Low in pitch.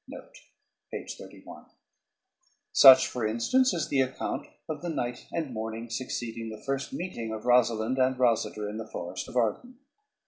Yes: low, 125 Hz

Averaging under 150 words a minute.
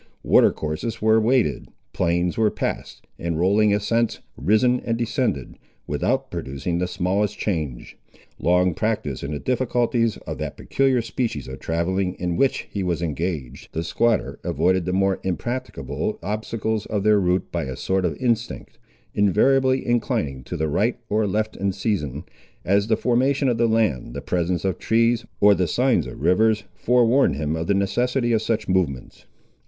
No: average, 165 wpm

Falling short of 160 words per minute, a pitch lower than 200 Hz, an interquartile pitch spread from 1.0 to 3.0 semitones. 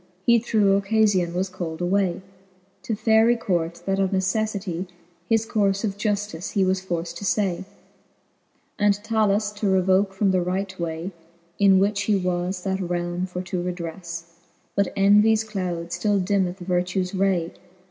Yes: average, 150 wpm; high, 190 Hz; narrow, 2.4 semitones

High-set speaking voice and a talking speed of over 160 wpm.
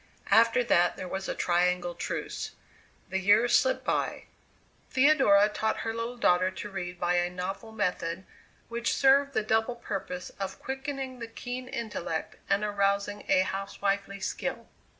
No: high, 205 Hz; average, 150 wpm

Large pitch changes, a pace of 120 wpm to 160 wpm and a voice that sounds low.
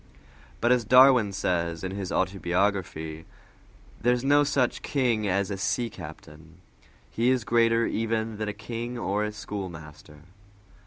No: average, 4.6 semitones; average, 145 wpm; low, 105 Hz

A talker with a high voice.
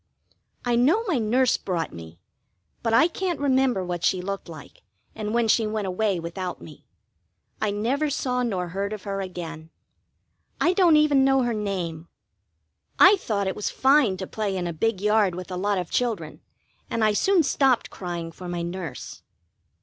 Yes: high, 205 Hz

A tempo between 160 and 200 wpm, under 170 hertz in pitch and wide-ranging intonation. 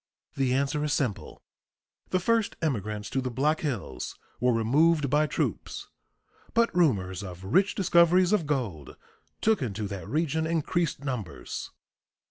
No: slow, 135 wpm; medium, 140 Hz; wide, 7.1 semitones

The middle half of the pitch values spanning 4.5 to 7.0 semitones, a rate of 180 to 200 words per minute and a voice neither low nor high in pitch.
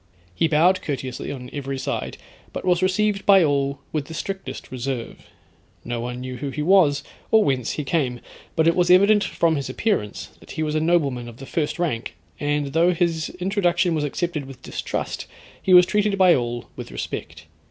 Yes: average, 5.1 semitones; average, 190 wpm; medium, 155 Hz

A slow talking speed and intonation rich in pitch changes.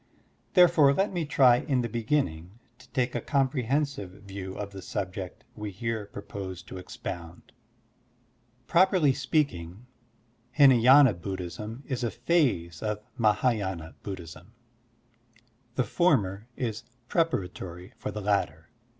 Yes: slow, 115 wpm; wide, 6.0 semitones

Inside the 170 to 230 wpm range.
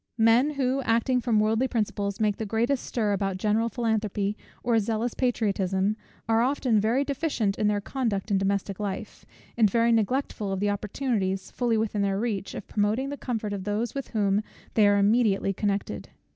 Yes: average, 175 wpm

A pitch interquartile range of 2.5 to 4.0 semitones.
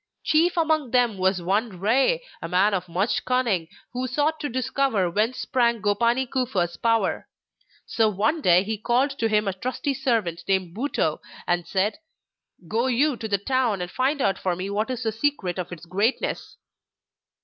No: average, 5.3 semitones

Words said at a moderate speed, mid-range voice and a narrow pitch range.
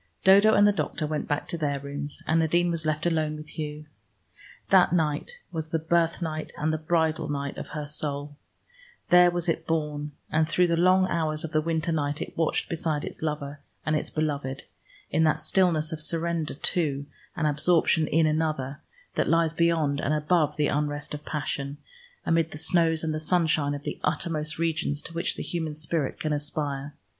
Yes: average, 185 wpm; medium, 155 Hz; narrow, 1.9 semitones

